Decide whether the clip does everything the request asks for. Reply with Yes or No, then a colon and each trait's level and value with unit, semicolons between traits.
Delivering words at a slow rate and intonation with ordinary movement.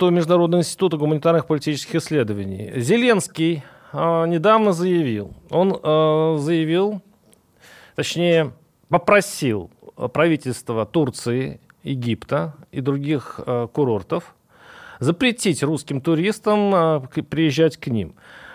Yes: slow, 90 wpm; average, 3.9 semitones